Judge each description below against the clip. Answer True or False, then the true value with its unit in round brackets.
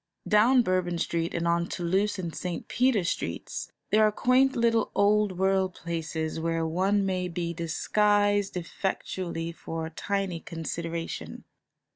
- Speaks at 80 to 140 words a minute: True (135 wpm)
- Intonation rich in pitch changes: False (3.5 semitones)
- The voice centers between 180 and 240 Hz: True (185 Hz)